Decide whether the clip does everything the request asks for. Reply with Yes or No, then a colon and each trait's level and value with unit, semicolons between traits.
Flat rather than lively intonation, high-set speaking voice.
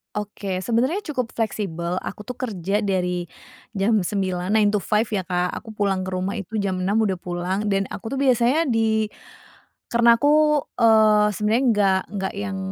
No: average, 3.1 semitones; high, 210 Hz